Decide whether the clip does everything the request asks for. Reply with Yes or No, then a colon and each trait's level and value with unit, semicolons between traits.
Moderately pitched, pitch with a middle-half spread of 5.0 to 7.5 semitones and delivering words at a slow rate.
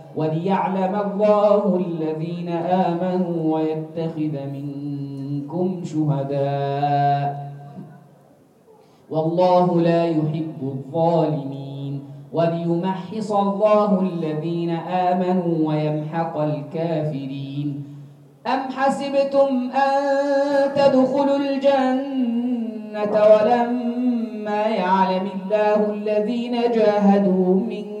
Yes: medium, 180 Hz; wide, 5.5 semitones; slow, 60 wpm